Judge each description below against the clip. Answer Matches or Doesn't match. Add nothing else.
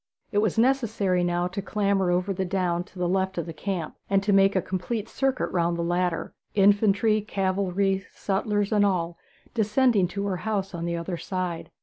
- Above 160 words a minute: Matches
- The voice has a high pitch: Matches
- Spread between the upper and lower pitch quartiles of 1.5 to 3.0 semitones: Matches